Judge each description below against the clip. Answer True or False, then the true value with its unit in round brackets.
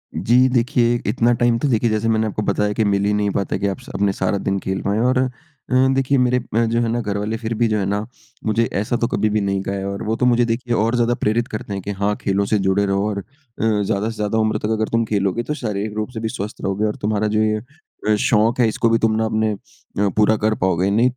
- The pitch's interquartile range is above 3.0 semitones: False (2.5 semitones)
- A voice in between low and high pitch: False (110 Hz)